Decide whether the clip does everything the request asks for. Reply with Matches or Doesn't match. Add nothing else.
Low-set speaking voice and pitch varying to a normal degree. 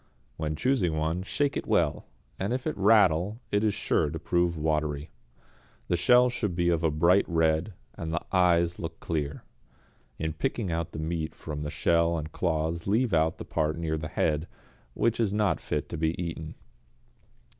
Matches